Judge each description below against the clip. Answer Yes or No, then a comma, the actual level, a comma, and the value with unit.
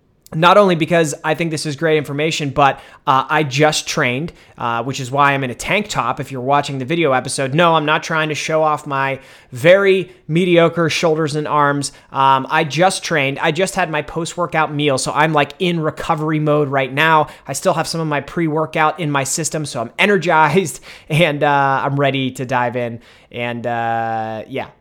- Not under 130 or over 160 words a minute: No, fast, 205 wpm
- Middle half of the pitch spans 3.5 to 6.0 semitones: No, average, 3.1 semitones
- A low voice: No, medium, 150 Hz